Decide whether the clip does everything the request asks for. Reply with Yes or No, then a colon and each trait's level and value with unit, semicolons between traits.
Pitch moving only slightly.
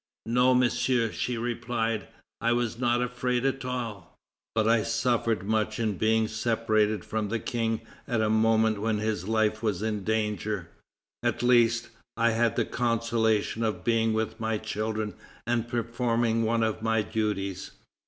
Yes: narrow, 1.3 semitones